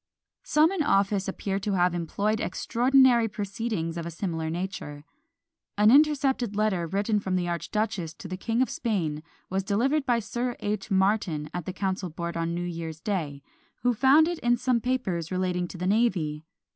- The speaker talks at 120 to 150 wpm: No, average, 175 wpm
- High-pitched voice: Yes, high, 195 Hz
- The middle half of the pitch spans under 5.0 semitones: No, wide, 5.4 semitones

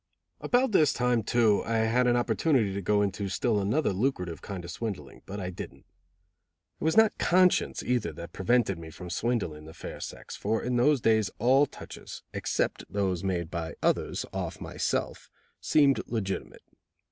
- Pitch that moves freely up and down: No, average, 4.7 semitones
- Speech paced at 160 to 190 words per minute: Yes, average, 165 wpm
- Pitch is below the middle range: Yes, low, 110 Hz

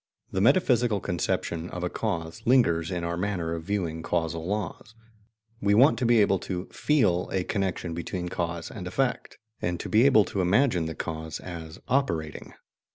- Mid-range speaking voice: No, very low, 90 Hz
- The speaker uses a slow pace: No, average, 170 wpm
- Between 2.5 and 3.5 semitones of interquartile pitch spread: No, average, 4.2 semitones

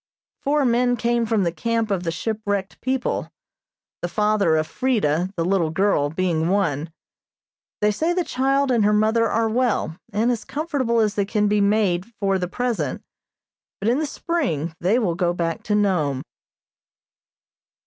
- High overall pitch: Yes, high, 210 Hz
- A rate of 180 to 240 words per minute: No, average, 165 wpm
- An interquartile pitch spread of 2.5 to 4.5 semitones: No, average, 5.2 semitones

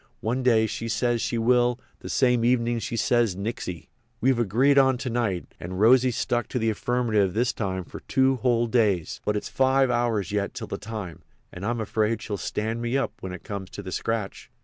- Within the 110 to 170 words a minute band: No, fast, 205 wpm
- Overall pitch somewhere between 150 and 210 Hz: No, low, 115 Hz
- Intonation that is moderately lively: Yes, average, 3.0 semitones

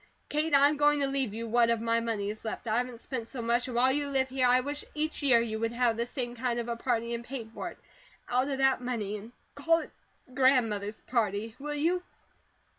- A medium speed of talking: No, fast, 240 wpm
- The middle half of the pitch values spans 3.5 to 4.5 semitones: No, average, 3.0 semitones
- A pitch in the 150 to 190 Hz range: No, high, 245 Hz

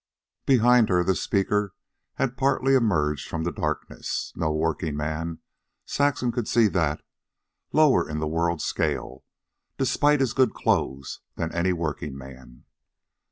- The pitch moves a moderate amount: No, wide, 8.1 semitones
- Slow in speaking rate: Yes, slow, 125 wpm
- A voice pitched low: Yes, very low, 85 Hz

